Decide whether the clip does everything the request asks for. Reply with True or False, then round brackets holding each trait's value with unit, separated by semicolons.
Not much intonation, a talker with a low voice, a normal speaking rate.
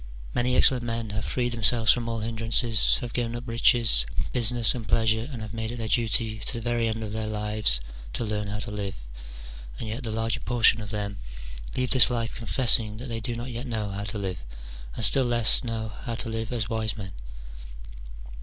False (1.8 semitones; 115 Hz; 210 wpm)